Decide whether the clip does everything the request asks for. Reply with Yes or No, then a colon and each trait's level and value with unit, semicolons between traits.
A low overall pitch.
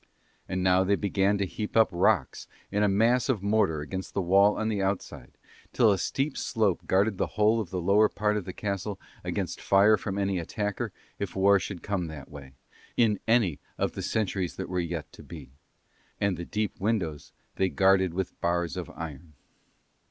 Yes: very low, 95 Hz